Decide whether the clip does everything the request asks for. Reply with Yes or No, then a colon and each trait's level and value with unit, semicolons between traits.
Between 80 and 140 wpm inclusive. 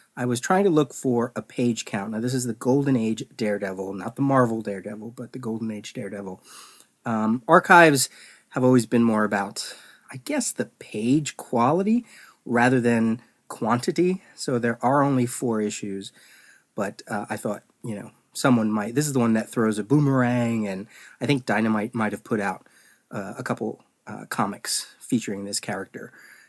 No: average, 175 wpm